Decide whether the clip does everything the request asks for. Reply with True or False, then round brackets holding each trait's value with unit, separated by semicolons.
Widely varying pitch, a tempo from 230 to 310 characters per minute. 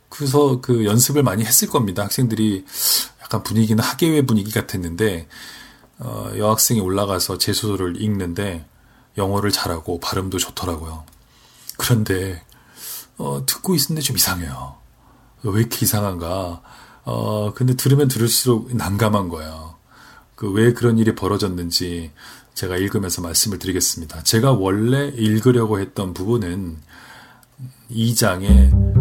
False (4.7 semitones; 300 characters per minute)